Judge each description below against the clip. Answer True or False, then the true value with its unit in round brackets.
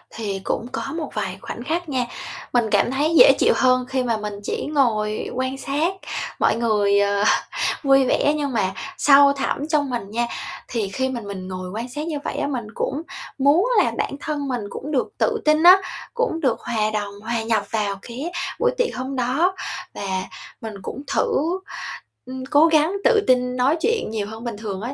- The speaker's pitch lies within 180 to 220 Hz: False (255 Hz)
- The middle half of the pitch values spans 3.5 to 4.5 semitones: False (5.4 semitones)